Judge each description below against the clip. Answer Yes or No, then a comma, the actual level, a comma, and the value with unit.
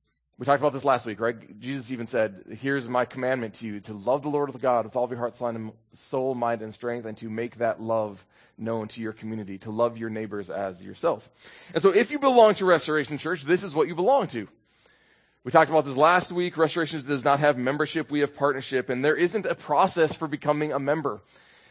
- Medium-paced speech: No, fast, 225 wpm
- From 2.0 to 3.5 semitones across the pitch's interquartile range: No, average, 5.1 semitones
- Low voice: Yes, low, 130 Hz